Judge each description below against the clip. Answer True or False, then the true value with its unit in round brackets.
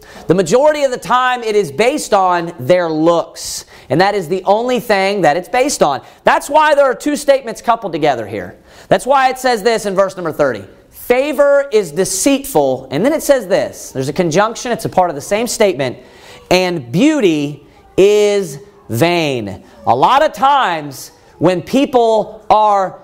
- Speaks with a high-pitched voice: True (200 Hz)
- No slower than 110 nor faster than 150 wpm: False (175 wpm)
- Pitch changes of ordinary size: False (6.7 semitones)